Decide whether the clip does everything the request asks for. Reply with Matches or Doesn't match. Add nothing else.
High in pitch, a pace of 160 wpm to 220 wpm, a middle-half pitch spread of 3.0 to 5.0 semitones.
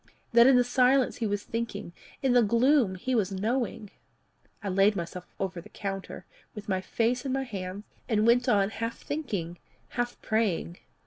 Matches